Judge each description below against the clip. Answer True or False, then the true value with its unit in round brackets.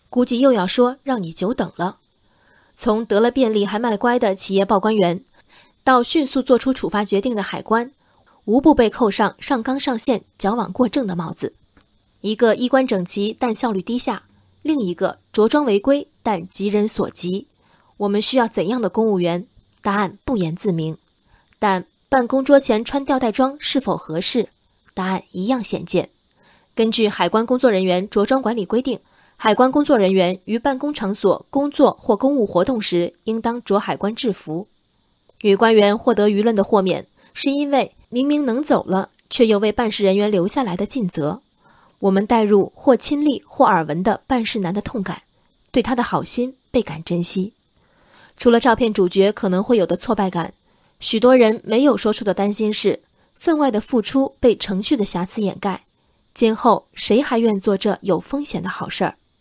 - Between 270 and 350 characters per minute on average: False (260 characters per minute)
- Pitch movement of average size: True (4.4 semitones)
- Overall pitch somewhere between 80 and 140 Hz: False (215 Hz)